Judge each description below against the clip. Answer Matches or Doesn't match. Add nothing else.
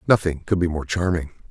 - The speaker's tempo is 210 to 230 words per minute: Doesn't match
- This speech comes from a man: Matches